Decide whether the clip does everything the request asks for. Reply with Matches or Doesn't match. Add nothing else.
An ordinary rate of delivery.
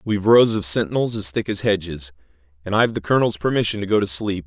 Doesn't match